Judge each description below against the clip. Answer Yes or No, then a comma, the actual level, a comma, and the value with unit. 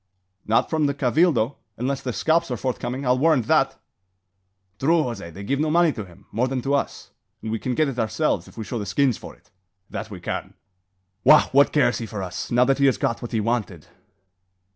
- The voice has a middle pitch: No, low, 125 Hz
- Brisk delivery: Yes, fast, 220 wpm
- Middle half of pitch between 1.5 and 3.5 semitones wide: No, average, 4.1 semitones